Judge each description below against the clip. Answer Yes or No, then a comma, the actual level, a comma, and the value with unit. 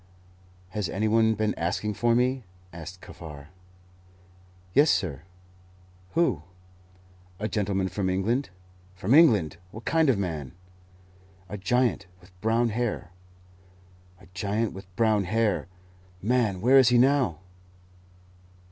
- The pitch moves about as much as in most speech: Yes, average, 4.4 semitones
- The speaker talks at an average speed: No, slow, 120 wpm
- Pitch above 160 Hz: No, low, 105 Hz